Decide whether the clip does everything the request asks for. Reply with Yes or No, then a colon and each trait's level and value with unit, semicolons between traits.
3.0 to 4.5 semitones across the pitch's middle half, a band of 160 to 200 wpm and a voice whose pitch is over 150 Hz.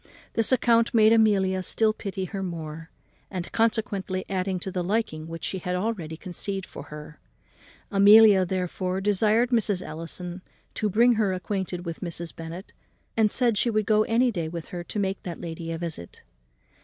Yes: average, 3.8 semitones; average, 170 wpm; high, 190 Hz